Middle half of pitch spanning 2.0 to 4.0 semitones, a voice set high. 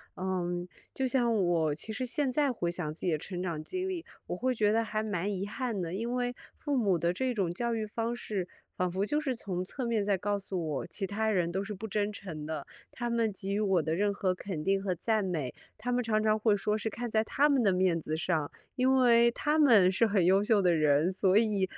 No: average, 4.5 semitones; high, 205 Hz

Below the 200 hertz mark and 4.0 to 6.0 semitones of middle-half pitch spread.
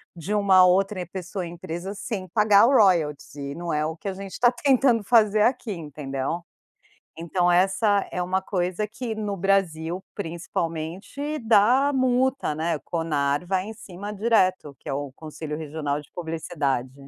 Yes: medium, 185 Hz; average, 4.7 semitones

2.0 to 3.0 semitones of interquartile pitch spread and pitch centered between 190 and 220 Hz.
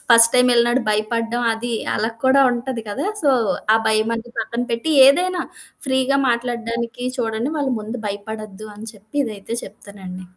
No: narrow, 2.5 semitones; high, 235 Hz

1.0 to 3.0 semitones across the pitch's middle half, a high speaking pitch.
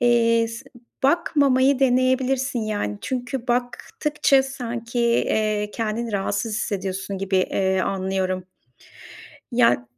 No: average, 4.5 semitones; high, 230 Hz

